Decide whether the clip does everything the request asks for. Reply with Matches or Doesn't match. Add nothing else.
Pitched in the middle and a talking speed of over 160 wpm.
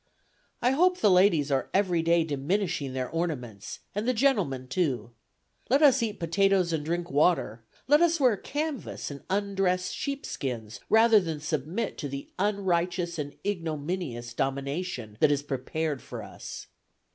Doesn't match